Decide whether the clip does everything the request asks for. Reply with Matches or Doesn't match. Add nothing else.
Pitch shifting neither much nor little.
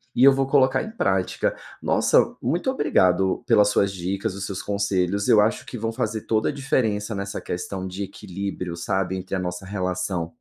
Matches